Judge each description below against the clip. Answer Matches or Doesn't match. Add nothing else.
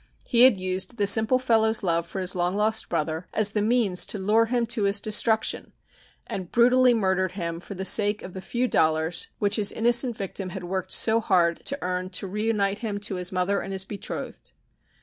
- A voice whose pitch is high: Matches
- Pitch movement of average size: Matches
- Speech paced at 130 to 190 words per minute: Doesn't match